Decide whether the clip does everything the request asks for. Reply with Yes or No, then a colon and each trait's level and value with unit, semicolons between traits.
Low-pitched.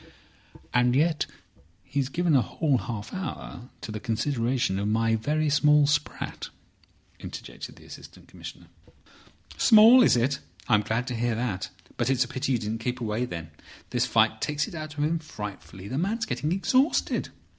Yes: low, 130 Hz